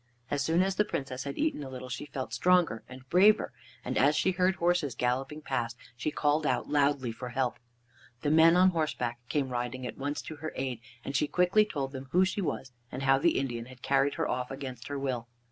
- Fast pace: Yes, fast, 220 wpm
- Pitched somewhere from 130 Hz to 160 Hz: Yes, medium, 140 Hz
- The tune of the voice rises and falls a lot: No, average, 4.0 semitones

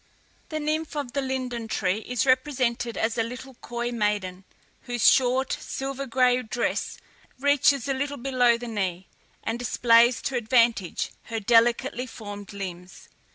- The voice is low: No, high, 240 Hz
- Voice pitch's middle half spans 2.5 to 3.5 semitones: Yes, average, 2.8 semitones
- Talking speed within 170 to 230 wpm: No, average, 145 wpm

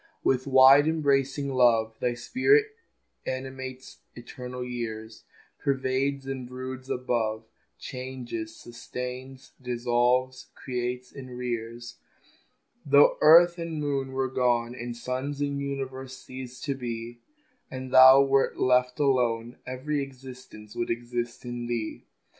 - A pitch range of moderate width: No, narrow, 1.9 semitones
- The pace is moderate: No, slow, 115 wpm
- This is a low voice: Yes, low, 130 Hz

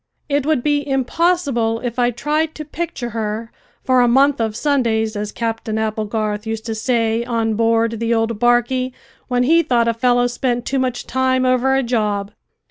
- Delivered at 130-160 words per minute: No, average, 180 wpm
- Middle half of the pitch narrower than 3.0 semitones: Yes, narrow, 2.6 semitones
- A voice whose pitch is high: Yes, high, 240 Hz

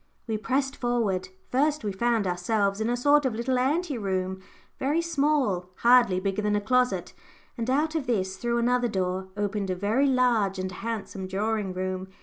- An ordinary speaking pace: Yes, average, 175 wpm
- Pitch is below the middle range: No, high, 225 Hz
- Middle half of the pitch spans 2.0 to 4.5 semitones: No, average, 4.9 semitones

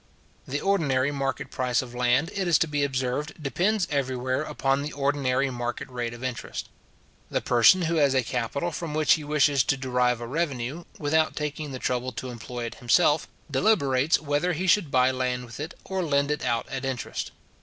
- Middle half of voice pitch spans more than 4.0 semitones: No, average, 3.2 semitones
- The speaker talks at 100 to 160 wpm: No, average, 190 wpm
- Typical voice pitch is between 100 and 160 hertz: Yes, low, 135 Hz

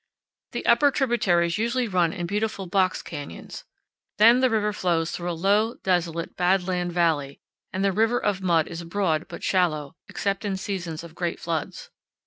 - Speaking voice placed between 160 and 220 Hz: Yes, medium, 185 Hz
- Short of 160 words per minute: No, average, 170 wpm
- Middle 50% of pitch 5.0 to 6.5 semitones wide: No, average, 3.5 semitones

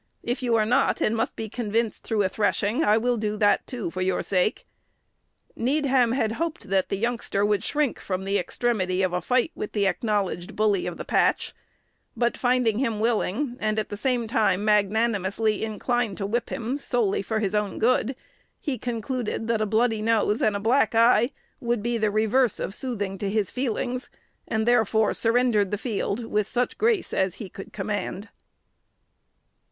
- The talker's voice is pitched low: No, high, 220 Hz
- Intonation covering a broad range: No, average, 2.9 semitones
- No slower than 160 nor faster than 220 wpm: Yes, average, 180 wpm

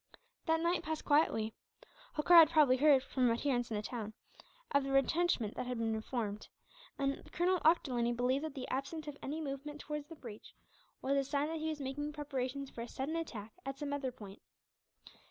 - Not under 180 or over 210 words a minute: Yes, average, 190 wpm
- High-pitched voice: Yes, very high, 275 Hz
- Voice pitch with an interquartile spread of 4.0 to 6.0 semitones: No, average, 3.6 semitones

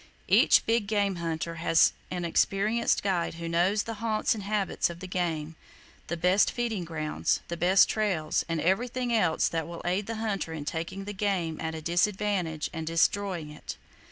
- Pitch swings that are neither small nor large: Yes, average, 3.9 semitones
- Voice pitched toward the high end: No, medium, 180 Hz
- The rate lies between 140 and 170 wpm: No, average, 180 wpm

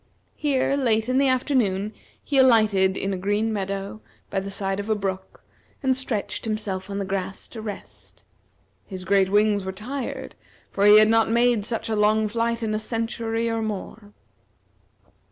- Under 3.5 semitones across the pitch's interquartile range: Yes, average, 2.7 semitones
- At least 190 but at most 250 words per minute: No, average, 170 wpm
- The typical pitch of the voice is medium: No, high, 215 Hz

